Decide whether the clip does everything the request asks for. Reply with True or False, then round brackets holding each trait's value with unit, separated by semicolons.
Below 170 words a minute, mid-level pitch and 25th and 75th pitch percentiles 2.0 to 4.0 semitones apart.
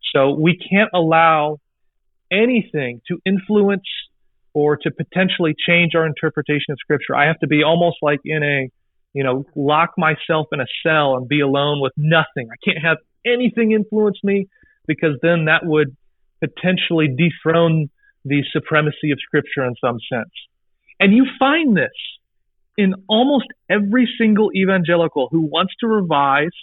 False (150 wpm; 160 Hz; 4.4 semitones)